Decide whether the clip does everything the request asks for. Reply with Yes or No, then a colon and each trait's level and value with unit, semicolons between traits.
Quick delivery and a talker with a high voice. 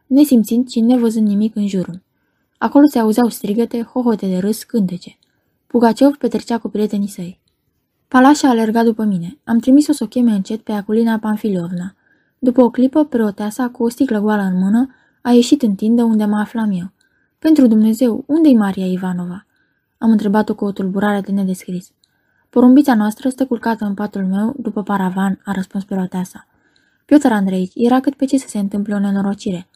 Yes: fast, 175 wpm; high, 220 Hz